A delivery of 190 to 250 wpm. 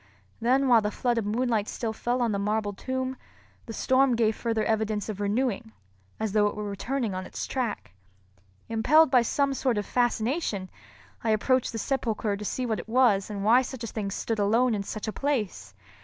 Yes: average, 200 wpm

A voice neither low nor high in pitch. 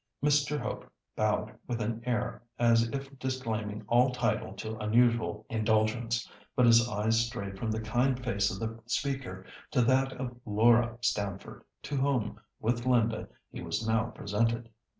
No: low, 115 Hz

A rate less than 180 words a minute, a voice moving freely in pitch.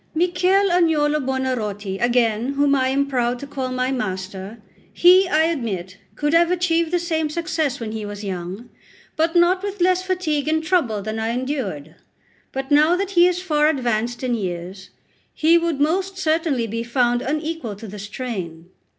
Yes: average, 170 wpm; wide, 6.9 semitones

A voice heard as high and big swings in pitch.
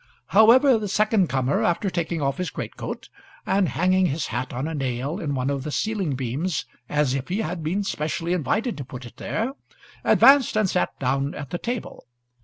No: medium, 165 Hz; wide, 6.5 semitones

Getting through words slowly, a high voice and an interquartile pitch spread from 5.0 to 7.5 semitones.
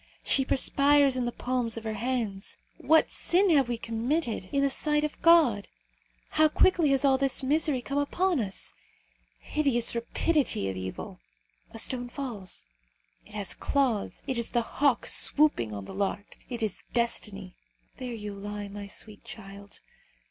No: average, 165 wpm; high, 245 Hz; average, 5.3 semitones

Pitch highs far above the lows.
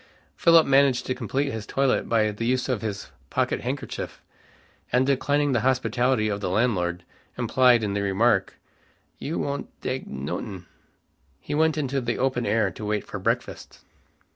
No: average, 4.2 semitones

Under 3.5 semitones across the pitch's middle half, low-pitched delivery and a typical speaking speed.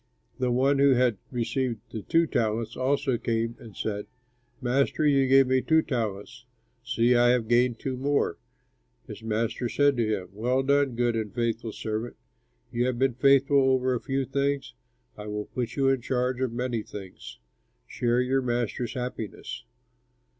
Yes: narrow, 2.6 semitones; low, 125 Hz; average, 165 wpm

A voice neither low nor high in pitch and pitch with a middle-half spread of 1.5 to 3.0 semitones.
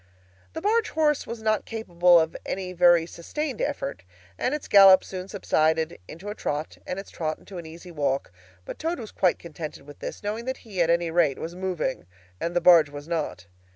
No: medium, 175 Hz; average, 4.5 semitones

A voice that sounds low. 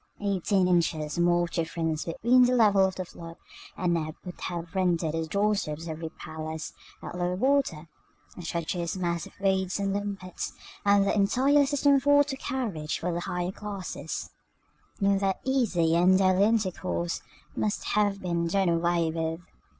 No: medium, 180 Hz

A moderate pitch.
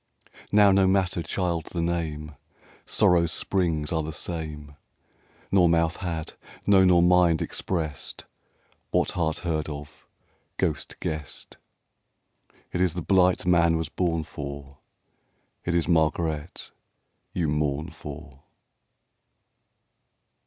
No: very low, 85 Hz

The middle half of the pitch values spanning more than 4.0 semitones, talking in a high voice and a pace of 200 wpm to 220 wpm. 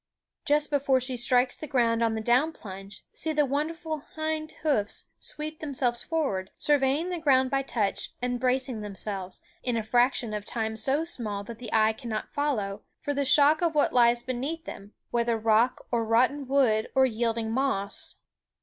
No: average, 4.5 semitones; very high, 250 Hz; average, 175 wpm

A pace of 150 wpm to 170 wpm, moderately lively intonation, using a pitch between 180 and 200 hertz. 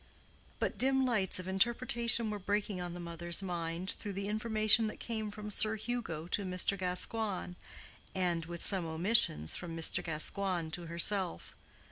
Yes: average, 155 wpm; average, 4.0 semitones; high, 190 Hz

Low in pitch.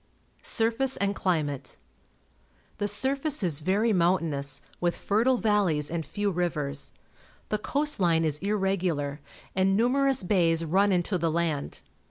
No: medium, 185 Hz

